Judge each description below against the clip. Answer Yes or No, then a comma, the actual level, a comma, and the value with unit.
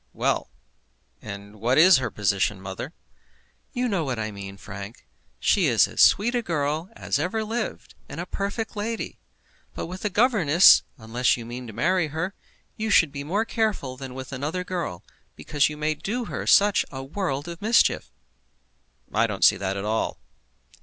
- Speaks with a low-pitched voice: No, medium, 150 Hz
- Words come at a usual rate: Yes, average, 175 wpm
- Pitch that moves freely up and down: Yes, wide, 8.7 semitones